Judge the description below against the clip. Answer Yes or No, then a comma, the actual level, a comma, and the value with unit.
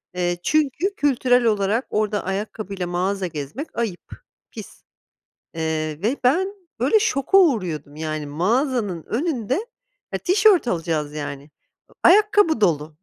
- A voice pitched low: No, high, 205 Hz